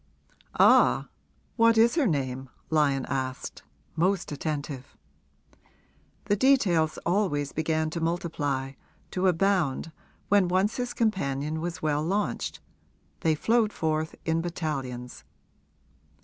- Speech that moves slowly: Yes, slow, 105 wpm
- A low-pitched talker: No, medium, 160 Hz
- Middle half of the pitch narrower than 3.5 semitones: No, average, 5.0 semitones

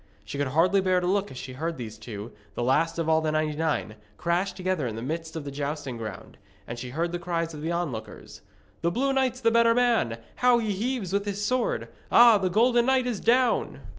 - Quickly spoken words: Yes, fast, 225 wpm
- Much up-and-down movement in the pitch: Yes, wide, 7.7 semitones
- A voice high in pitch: No, medium, 170 Hz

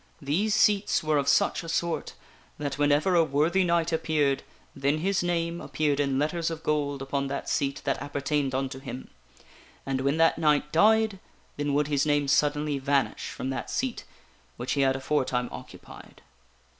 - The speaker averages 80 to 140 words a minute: No, average, 170 wpm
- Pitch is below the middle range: No, medium, 145 Hz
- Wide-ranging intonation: No, average, 2.9 semitones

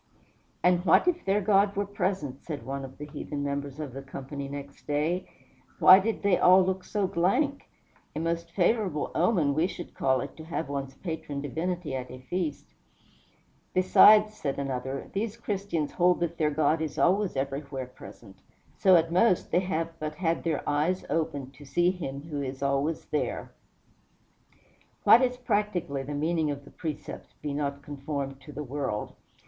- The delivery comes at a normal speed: Yes, average, 175 wpm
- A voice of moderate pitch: Yes, medium, 155 Hz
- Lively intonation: No, average, 4.7 semitones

